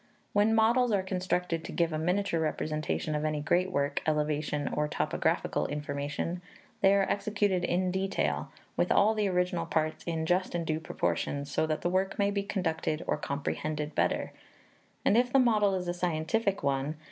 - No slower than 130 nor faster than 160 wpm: No, average, 180 wpm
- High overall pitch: No, medium, 175 Hz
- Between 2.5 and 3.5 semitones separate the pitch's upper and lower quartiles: No, average, 4.3 semitones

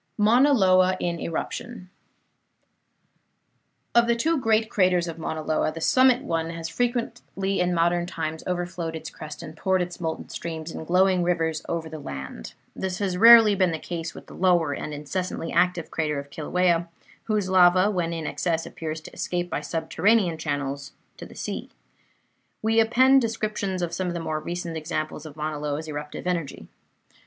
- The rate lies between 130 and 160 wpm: No, average, 170 wpm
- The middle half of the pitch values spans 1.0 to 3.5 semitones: Yes, average, 3.1 semitones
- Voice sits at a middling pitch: Yes, medium, 175 Hz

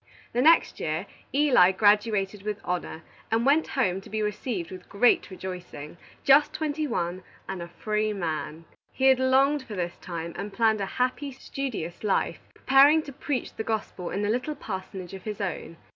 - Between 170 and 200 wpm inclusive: Yes, average, 175 wpm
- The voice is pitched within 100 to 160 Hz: No, high, 210 Hz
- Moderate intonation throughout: No, wide, 6.0 semitones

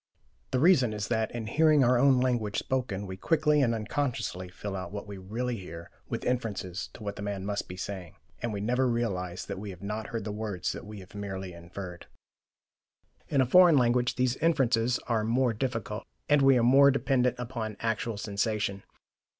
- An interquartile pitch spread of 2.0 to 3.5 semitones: No, average, 4.0 semitones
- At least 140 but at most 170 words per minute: No, average, 190 wpm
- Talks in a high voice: No, low, 110 Hz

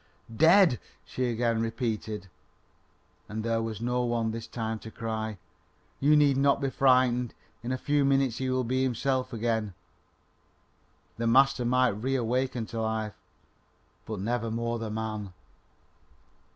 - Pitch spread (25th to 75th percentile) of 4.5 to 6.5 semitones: No, narrow, 2.6 semitones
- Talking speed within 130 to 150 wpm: Yes, average, 140 wpm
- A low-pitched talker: Yes, low, 120 Hz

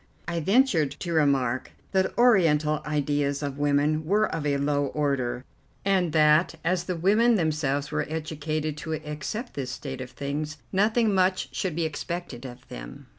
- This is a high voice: No, medium, 155 Hz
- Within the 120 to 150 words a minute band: No, average, 160 wpm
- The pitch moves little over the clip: No, average, 3.8 semitones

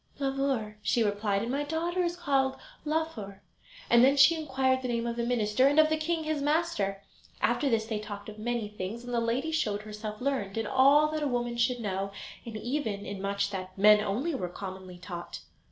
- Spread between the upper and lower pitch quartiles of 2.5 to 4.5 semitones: No, average, 5.3 semitones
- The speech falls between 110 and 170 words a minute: No, fast, 205 wpm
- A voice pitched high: Yes, high, 235 Hz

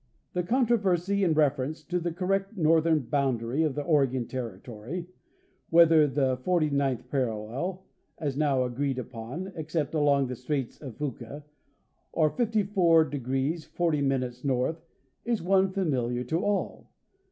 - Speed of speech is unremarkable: No, slow, 130 wpm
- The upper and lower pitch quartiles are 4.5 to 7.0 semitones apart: Yes, average, 5.0 semitones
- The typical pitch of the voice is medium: Yes, medium, 150 Hz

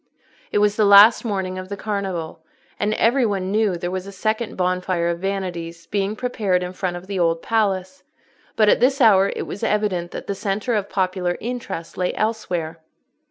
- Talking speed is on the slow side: No, average, 190 wpm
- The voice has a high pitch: Yes, high, 195 Hz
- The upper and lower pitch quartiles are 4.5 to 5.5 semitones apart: No, average, 2.8 semitones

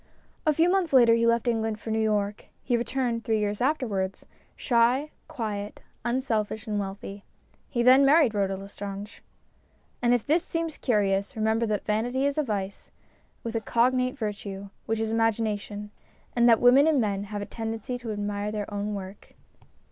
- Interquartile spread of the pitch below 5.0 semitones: Yes, average, 3.1 semitones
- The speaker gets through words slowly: No, average, 170 wpm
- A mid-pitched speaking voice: No, high, 225 Hz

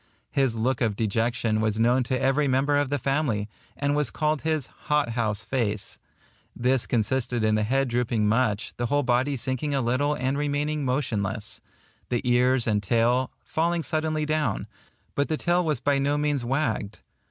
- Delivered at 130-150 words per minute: No, average, 175 wpm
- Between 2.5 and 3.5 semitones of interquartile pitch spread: No, average, 3.9 semitones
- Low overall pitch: Yes, low, 130 Hz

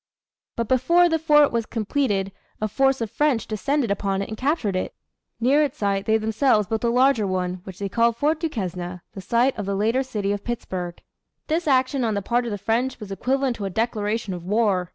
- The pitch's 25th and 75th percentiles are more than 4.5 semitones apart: Yes, average, 4.9 semitones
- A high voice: Yes, high, 225 Hz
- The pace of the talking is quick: Yes, fast, 215 wpm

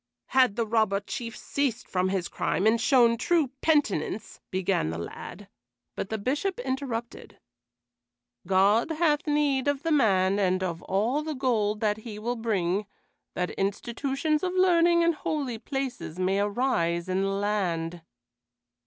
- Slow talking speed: No, average, 145 wpm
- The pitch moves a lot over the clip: Yes, wide, 6.1 semitones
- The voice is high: Yes, high, 225 Hz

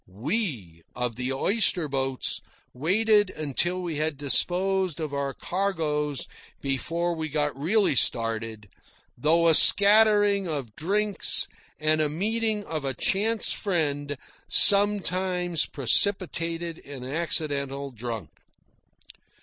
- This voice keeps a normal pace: No, slow, 110 wpm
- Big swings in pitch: Yes, wide, 5.7 semitones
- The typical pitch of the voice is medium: Yes, medium, 160 Hz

